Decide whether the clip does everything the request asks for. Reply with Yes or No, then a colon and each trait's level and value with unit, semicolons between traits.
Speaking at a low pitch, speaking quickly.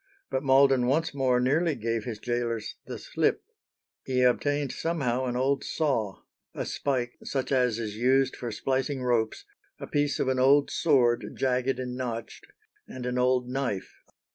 No: low, 130 Hz; average, 160 wpm